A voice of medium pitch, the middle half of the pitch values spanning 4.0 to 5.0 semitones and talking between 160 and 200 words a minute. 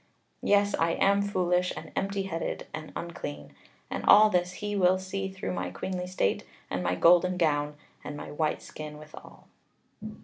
Yes: medium, 180 Hz; average, 4.3 semitones; average, 165 wpm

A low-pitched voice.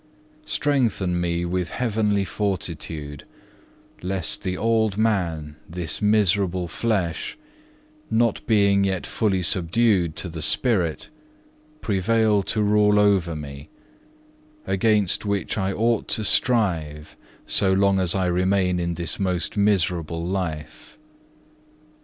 Yes: very low, 95 Hz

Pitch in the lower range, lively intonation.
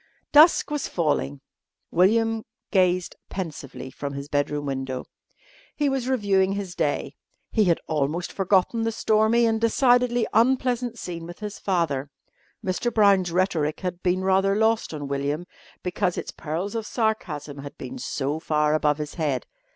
No: medium, 185 Hz; wide, 6.7 semitones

